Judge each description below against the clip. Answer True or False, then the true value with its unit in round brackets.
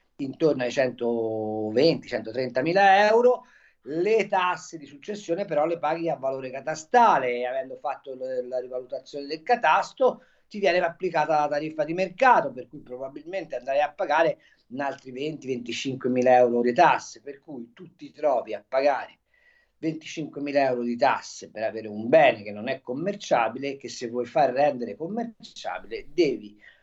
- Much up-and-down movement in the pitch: True (6.1 semitones)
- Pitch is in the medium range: True (145 Hz)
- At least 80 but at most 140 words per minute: False (155 wpm)